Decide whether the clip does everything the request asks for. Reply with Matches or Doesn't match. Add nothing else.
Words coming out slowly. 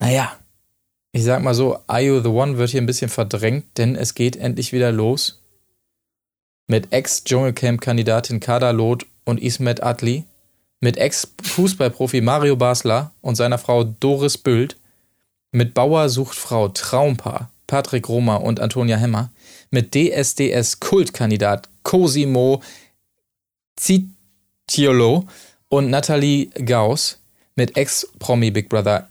Matches